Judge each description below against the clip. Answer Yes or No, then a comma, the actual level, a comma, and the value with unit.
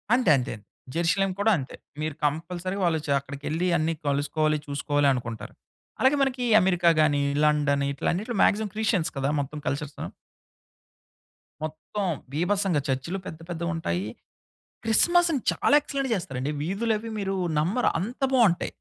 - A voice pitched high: No, medium, 165 Hz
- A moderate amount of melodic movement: No, wide, 6.0 semitones